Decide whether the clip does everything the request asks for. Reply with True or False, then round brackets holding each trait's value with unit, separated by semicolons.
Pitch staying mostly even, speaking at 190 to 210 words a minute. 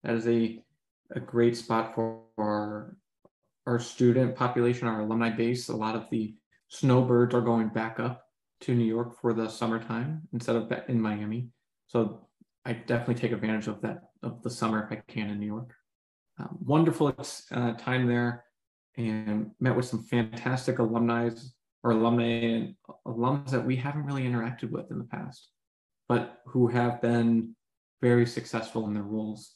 False (1.5 semitones; 165 wpm)